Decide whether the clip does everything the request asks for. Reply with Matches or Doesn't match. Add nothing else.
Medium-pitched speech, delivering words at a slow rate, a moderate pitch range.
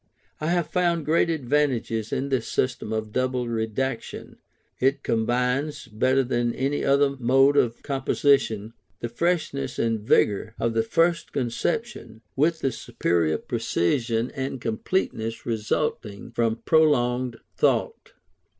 Doesn't match